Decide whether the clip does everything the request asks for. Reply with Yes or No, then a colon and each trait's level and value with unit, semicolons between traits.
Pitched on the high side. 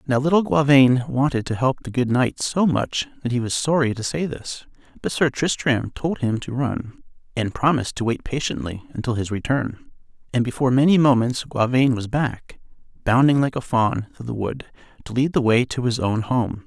No: low, 125 Hz